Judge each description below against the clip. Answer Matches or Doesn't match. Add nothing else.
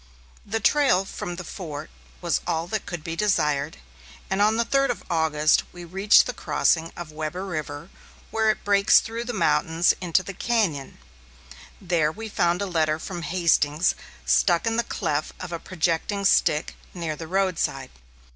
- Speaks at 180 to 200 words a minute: Doesn't match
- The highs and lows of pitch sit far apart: Doesn't match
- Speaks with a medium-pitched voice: Matches